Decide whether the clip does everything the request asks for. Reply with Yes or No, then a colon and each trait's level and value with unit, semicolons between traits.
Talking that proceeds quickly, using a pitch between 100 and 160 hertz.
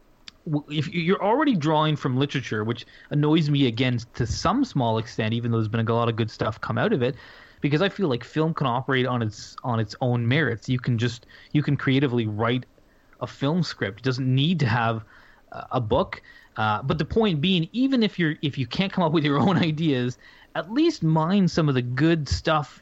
Yes: fast, 215 wpm; medium, 140 Hz